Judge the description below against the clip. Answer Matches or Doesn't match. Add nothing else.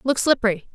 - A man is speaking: Doesn't match